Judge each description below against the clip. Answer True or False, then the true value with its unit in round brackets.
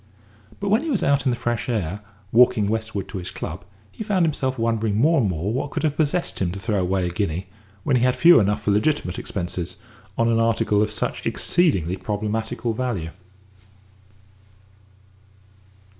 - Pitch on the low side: True (110 Hz)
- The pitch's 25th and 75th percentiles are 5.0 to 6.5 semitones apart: True (5.3 semitones)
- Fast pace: False (175 wpm)